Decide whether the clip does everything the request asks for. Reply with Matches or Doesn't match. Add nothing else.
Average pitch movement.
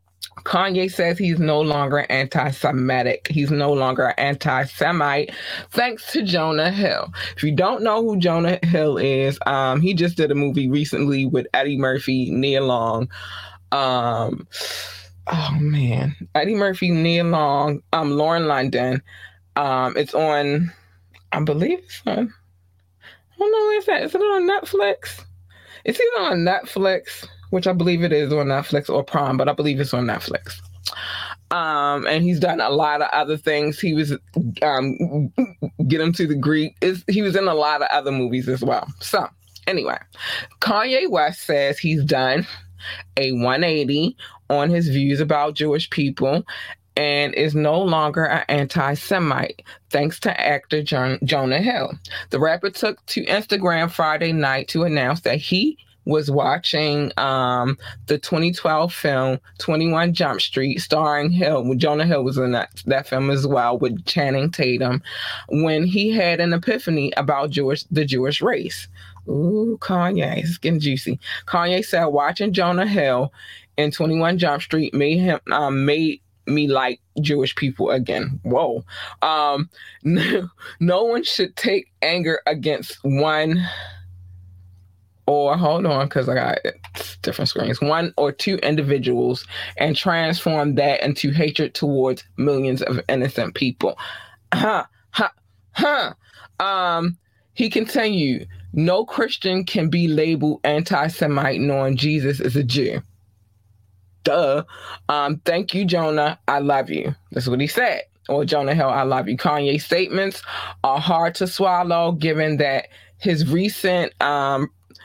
Matches